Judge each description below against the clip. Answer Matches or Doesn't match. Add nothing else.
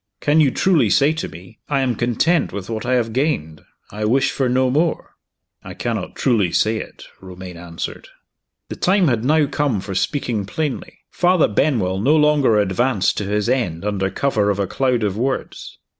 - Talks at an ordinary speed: Matches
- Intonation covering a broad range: Matches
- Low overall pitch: Matches